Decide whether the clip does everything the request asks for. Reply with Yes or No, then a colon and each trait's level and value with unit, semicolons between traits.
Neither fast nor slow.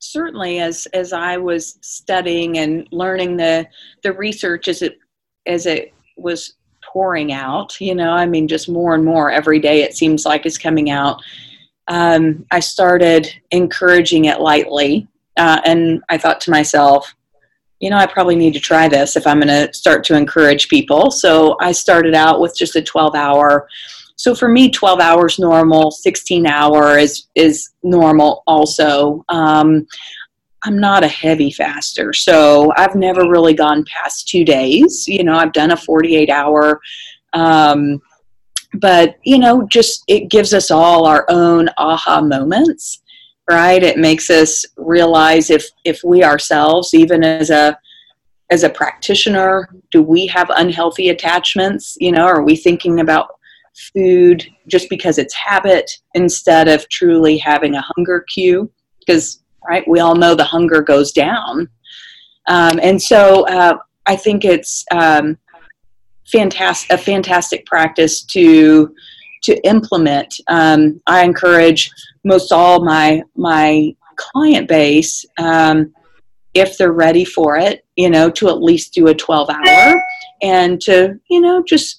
Yes: average, 150 wpm